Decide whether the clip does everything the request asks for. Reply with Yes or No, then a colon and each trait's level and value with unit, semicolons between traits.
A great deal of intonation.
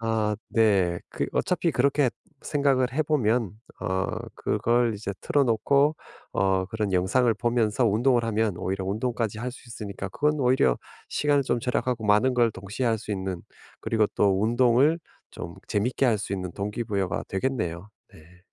No: average, 4.1 semitones